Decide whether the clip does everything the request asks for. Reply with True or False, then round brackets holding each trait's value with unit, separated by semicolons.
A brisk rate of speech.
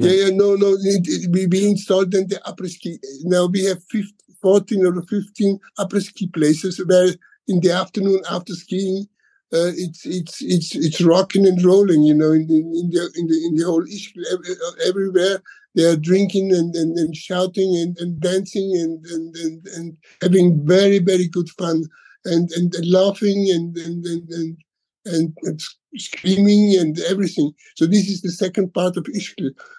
True (175 wpm)